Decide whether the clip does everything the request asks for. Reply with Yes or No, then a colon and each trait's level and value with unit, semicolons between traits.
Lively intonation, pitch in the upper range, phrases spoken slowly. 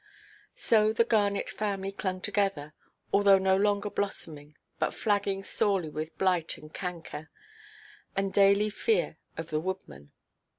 No: average, 3.7 semitones; high, 195 Hz; slow, 130 wpm